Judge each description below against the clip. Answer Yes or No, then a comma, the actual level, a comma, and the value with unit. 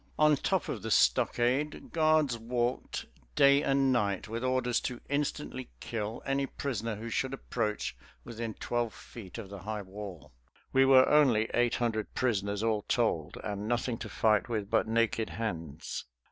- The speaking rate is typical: Yes, average, 160 wpm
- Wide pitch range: No, average, 3.5 semitones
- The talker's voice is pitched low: Yes, low, 115 Hz